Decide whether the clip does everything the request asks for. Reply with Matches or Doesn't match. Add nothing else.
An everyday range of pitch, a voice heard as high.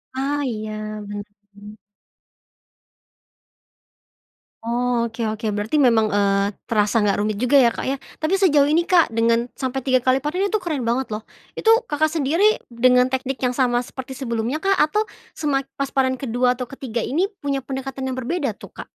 Matches